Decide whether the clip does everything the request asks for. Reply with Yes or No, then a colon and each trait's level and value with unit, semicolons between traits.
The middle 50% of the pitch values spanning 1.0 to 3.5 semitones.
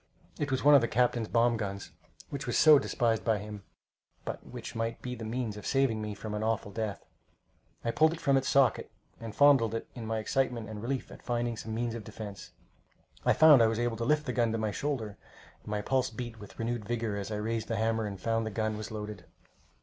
Yes: narrow, 2.4 semitones